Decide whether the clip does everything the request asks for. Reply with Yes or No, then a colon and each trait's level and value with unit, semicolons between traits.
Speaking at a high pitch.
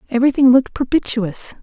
Yes: very high, 250 Hz